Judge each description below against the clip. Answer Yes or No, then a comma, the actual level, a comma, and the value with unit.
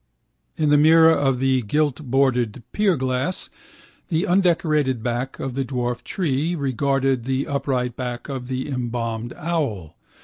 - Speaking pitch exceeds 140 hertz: No, low, 135 Hz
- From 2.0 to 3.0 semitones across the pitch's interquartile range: No, average, 3.5 semitones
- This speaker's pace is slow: Yes, slow, 130 wpm